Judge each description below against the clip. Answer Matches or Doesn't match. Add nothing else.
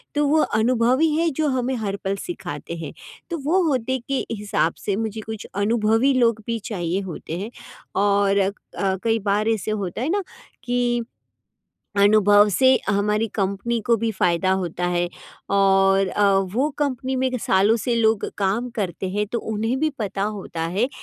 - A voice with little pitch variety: Doesn't match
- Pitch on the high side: Matches